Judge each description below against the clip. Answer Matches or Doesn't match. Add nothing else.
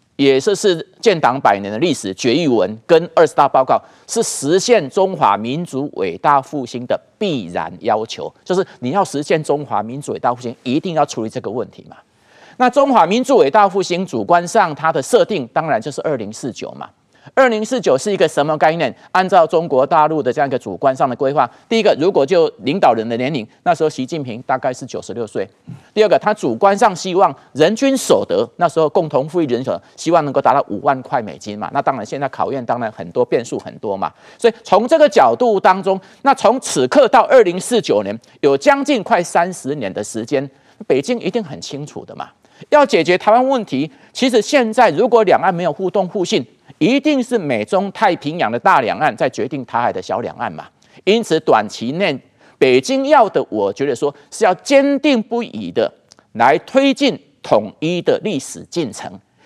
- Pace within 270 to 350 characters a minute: Matches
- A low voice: Doesn't match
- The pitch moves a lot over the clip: Matches